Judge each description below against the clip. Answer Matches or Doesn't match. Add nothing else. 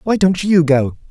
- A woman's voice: Doesn't match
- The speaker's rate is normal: Doesn't match